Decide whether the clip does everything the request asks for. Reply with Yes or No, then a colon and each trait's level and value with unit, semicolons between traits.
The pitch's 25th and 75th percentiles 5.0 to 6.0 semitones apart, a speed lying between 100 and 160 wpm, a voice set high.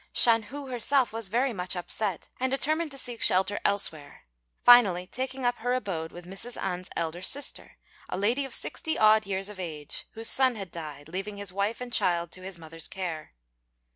No: wide, 5.4 semitones; average, 190 wpm; high, 200 Hz